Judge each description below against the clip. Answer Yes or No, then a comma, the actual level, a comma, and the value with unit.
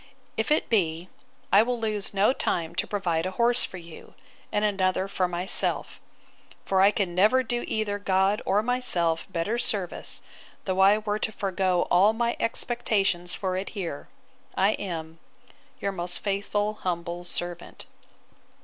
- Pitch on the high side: Yes, high, 195 Hz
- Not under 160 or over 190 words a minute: No, average, 150 wpm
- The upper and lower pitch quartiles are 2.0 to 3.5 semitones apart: Yes, average, 3.2 semitones